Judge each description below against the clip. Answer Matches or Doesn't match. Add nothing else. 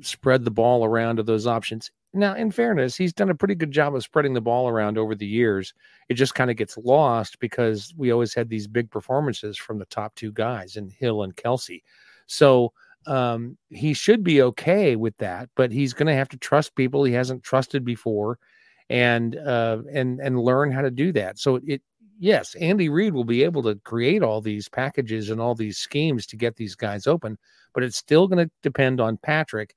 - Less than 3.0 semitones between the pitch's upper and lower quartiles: Doesn't match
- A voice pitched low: Matches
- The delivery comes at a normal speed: Doesn't match